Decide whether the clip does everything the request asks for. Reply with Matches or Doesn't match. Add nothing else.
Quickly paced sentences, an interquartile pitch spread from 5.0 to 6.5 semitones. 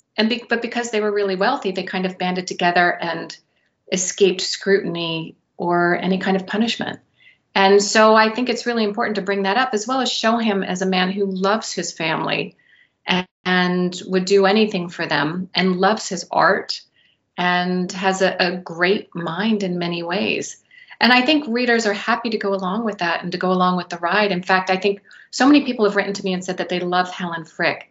Doesn't match